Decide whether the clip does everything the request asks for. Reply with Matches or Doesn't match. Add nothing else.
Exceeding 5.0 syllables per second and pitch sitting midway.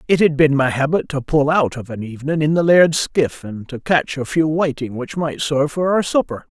Matches